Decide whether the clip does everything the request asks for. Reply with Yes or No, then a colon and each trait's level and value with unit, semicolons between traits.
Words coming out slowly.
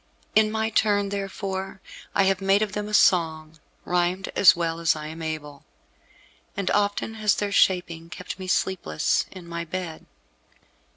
No: average, 160 wpm